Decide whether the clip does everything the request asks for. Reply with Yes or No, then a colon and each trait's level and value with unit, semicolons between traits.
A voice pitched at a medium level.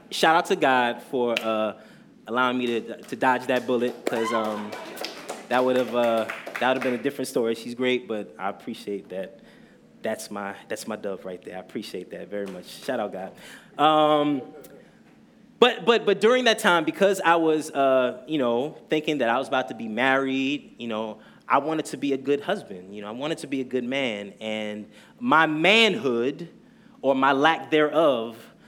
No: low, 130 Hz